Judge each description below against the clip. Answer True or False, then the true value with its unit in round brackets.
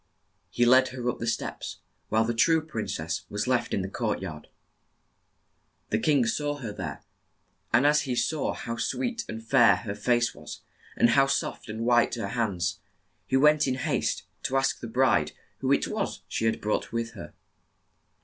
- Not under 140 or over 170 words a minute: False (185 wpm)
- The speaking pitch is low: True (120 Hz)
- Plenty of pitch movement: False (3.2 semitones)